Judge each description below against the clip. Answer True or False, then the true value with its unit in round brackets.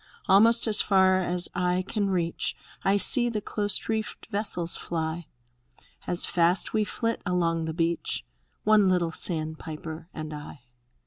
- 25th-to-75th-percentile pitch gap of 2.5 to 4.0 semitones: True (3.6 semitones)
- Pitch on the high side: False (180 Hz)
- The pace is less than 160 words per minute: True (145 wpm)